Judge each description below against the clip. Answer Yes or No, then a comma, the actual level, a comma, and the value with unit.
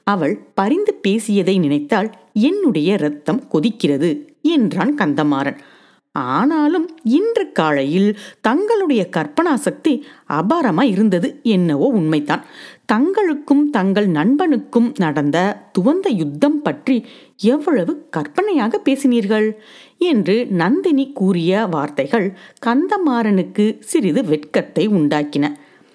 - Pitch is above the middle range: Yes, high, 230 Hz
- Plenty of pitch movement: Yes, wide, 7.8 semitones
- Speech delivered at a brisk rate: No, average, 85 wpm